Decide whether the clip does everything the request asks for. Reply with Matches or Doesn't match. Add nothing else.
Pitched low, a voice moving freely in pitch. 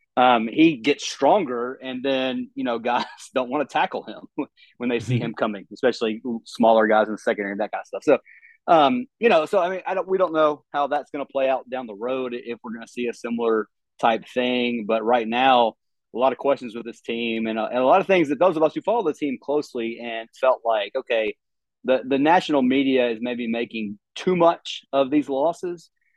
Matches